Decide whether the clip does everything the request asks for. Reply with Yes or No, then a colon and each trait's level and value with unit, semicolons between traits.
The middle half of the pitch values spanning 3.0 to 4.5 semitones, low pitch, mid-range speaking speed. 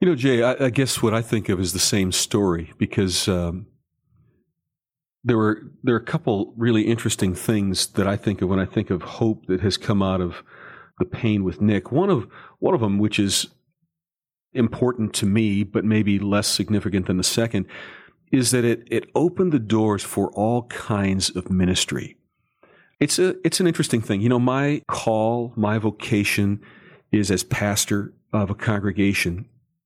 Yes: average, 3.6 semitones; low, 110 Hz; average, 180 wpm